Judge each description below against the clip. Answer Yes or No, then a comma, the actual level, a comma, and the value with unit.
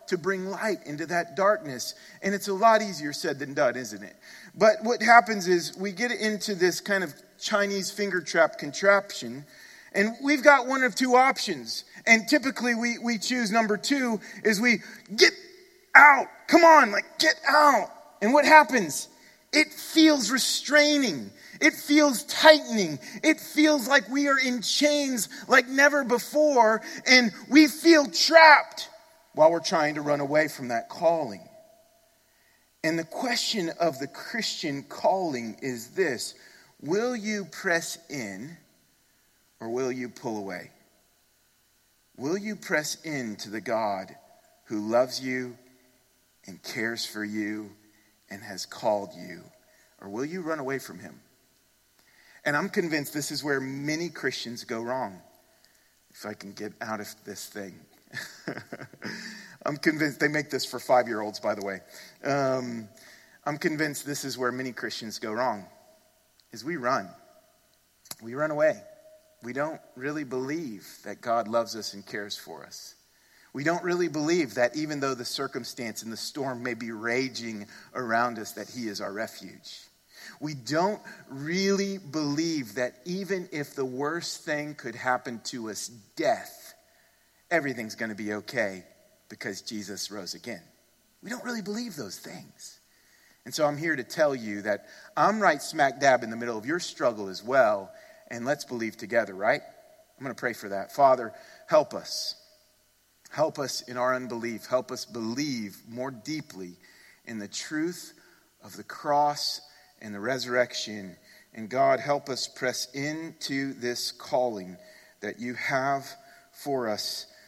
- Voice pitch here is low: No, medium, 155 Hz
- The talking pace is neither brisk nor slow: Yes, average, 155 wpm